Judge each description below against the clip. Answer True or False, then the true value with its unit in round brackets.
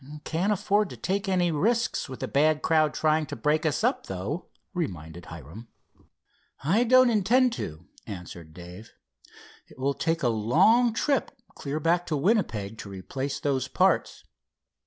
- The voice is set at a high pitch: False (155 Hz)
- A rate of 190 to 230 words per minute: False (155 wpm)